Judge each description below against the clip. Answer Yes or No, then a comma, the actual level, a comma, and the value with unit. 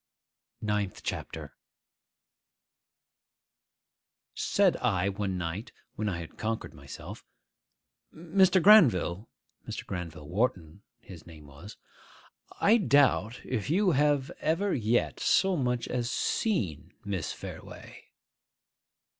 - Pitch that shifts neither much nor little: No, wide, 8.4 semitones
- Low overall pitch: Yes, low, 110 Hz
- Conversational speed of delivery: No, slow, 95 wpm